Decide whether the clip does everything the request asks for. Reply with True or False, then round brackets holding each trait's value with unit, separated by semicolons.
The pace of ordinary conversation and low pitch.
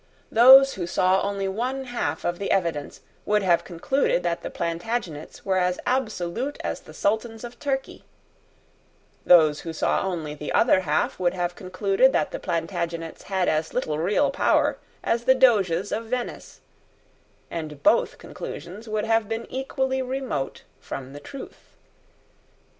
False (150 wpm; 195 Hz)